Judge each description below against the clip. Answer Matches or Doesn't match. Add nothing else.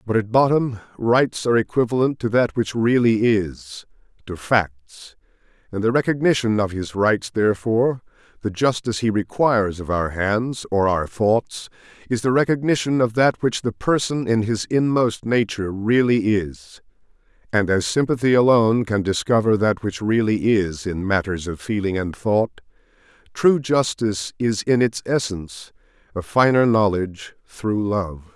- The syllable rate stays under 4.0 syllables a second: Doesn't match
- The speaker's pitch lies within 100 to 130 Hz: Matches